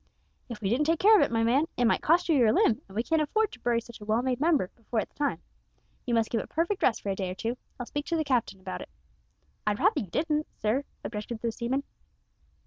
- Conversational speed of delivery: No, fast, 260 wpm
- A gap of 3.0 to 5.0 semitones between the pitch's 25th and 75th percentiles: No, wide, 5.4 semitones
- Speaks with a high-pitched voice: Yes, high, 240 Hz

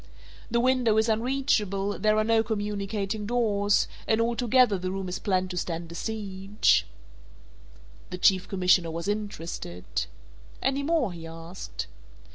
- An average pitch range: Yes, average, 3.6 semitones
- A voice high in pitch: Yes, high, 205 Hz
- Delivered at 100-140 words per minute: Yes, slow, 135 wpm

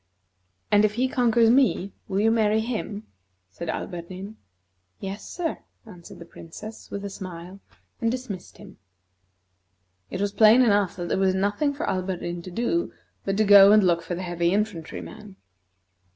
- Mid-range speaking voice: No, high, 200 Hz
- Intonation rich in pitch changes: No, average, 3.3 semitones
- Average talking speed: Yes, average, 165 wpm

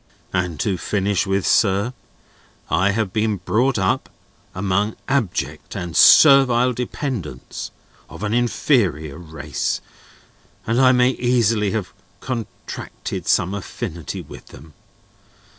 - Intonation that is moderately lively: Yes, average, 5.0 semitones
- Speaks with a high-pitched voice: No, low, 105 Hz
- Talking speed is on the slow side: Yes, slow, 110 wpm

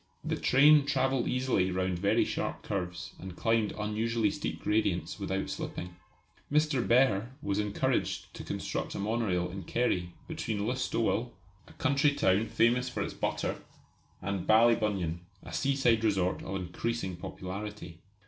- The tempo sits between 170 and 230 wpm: No, average, 140 wpm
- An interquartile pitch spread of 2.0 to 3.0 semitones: No, average, 4.3 semitones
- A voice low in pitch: Yes, low, 105 Hz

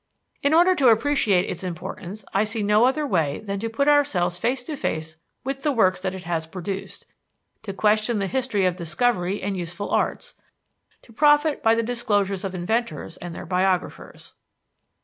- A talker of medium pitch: No, high, 205 Hz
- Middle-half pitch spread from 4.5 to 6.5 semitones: Yes, average, 5.0 semitones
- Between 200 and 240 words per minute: No, average, 175 wpm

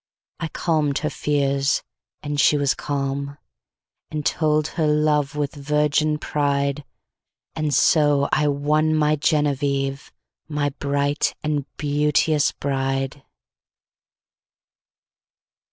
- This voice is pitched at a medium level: Yes, medium, 145 Hz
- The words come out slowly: Yes, slow, 90 wpm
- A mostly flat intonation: Yes, narrow, 1.3 semitones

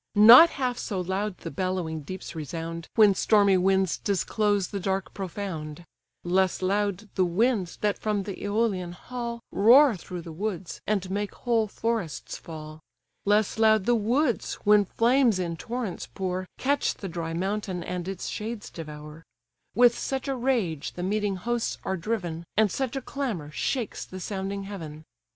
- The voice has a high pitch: Yes, high, 195 Hz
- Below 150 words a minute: No, average, 160 wpm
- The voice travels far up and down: No, average, 3.8 semitones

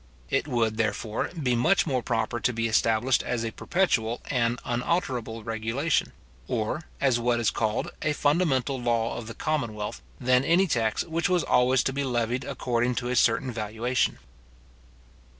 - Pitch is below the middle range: Yes, low, 120 Hz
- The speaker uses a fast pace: No, average, 160 wpm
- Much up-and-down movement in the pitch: No, average, 3.0 semitones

